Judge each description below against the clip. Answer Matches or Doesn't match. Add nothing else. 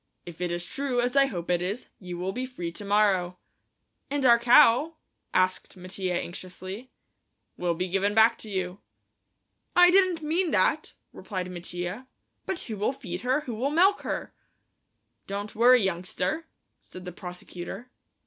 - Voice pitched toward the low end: Doesn't match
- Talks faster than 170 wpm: Doesn't match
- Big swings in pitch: Matches